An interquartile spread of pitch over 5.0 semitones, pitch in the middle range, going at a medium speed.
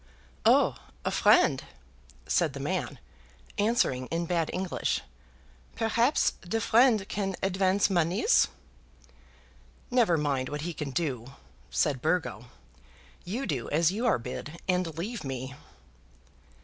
No: wide, 5.6 semitones; medium, 175 Hz; slow, 120 wpm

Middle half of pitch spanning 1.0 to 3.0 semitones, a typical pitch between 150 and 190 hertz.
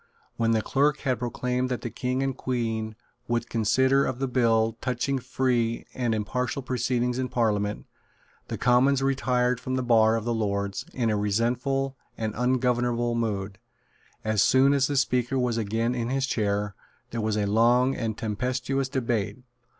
No: narrow, 2.5 semitones; low, 120 Hz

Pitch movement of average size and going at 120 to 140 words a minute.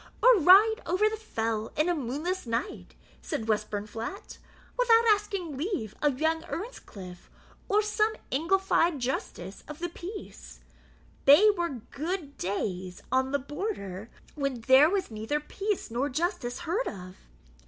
No: wide, 9.0 semitones; slow, 135 wpm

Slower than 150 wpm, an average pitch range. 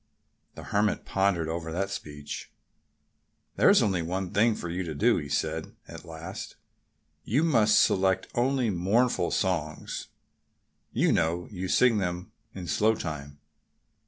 Yes: slow, 135 wpm; average, 4.3 semitones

